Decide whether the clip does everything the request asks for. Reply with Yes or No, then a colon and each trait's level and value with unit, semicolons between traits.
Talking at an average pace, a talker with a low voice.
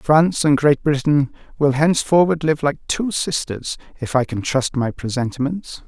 No: average, 165 wpm; medium, 145 Hz